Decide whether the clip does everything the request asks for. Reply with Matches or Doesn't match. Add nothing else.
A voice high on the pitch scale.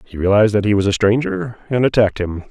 Doesn't match